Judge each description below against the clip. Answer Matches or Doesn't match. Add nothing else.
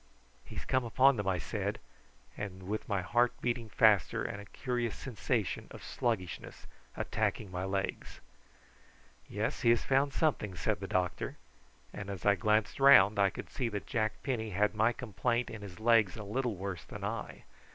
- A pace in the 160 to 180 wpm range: Matches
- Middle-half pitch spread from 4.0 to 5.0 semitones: Doesn't match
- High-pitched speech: Doesn't match